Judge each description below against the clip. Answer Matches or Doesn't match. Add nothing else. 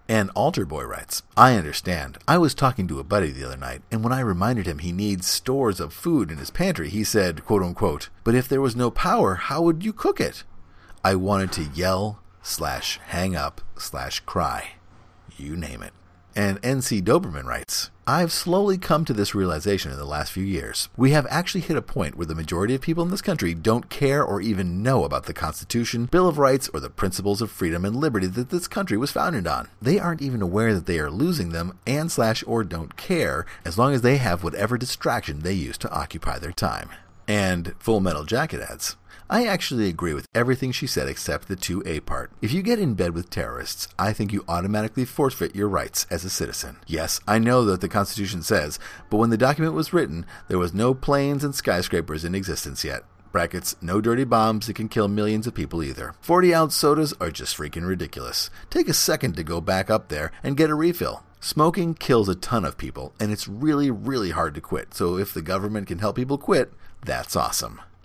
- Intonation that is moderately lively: Doesn't match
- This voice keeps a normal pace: Doesn't match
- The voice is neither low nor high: Doesn't match